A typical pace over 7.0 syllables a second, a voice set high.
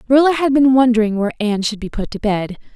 Yes: 7.4 syllables/s; high, 235 Hz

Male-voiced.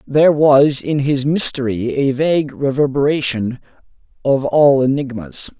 Yes: male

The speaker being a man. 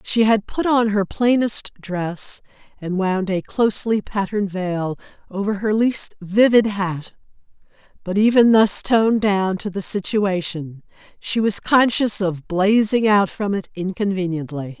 No: female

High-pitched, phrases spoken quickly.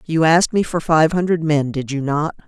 No: medium, 160 Hz; fast, 240 wpm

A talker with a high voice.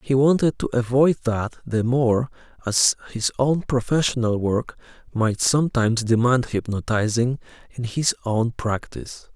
No: low, 120 Hz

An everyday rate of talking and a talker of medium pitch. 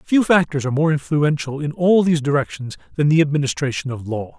Yes: average, 190 wpm; medium, 150 Hz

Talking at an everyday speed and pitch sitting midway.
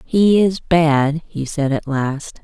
Yes: average, 170 wpm; medium, 155 Hz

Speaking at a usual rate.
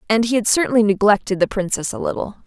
No: fast, 220 wpm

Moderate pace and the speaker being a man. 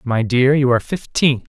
Yes: average, 195 wpm; male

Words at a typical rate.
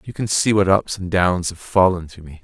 No: fast, 270 wpm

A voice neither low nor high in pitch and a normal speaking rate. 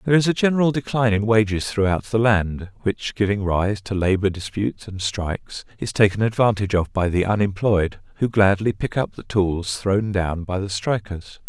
No: low, 105 Hz; average, 190 wpm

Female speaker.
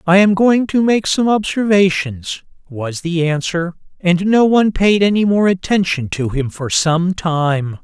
No: male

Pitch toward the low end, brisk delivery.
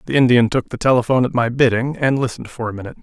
Yes: low, 120 Hz; fast, 260 wpm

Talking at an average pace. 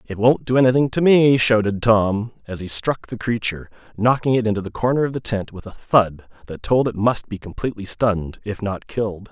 No: fast, 220 wpm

